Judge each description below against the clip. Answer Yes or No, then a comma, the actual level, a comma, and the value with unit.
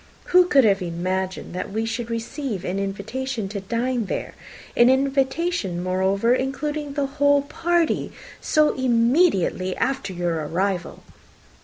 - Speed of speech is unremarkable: No, slow, 130 wpm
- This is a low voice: No, high, 230 Hz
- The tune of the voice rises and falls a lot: Yes, wide, 6.4 semitones